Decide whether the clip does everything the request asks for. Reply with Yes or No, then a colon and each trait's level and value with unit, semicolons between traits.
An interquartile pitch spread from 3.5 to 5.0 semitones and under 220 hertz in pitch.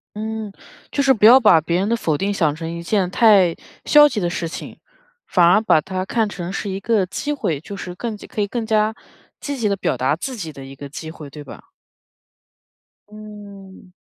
Yes: average, 4.4 semitones; high, 195 Hz